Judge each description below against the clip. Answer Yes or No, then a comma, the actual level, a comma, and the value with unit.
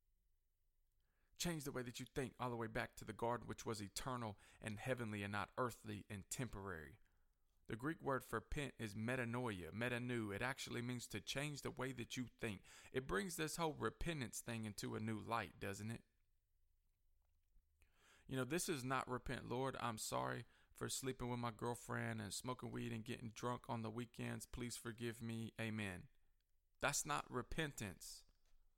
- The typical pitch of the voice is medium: No, low, 115 Hz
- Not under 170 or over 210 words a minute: Yes, average, 175 wpm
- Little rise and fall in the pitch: No, average, 4.3 semitones